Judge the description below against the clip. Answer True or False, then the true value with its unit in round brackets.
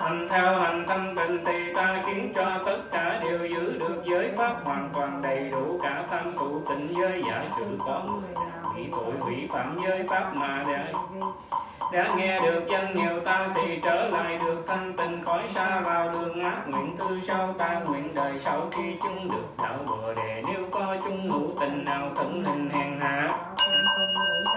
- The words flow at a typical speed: True (190 wpm)